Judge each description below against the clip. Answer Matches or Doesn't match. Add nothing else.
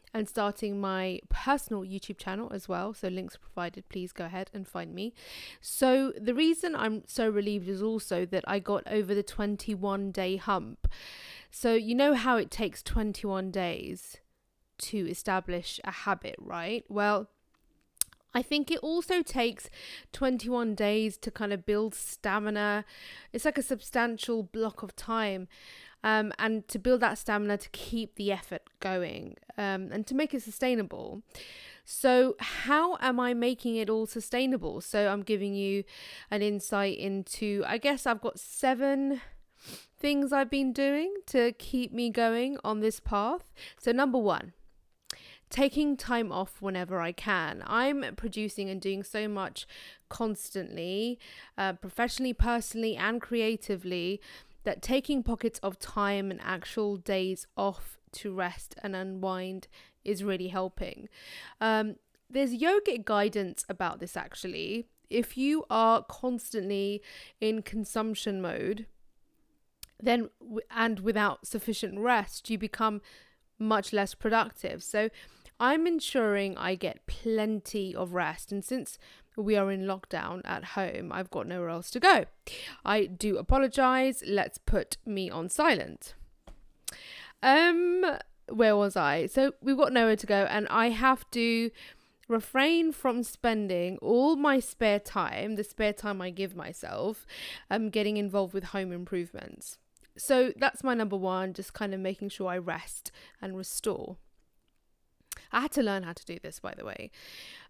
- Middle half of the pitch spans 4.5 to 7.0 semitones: Doesn't match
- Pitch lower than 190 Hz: Doesn't match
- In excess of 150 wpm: Doesn't match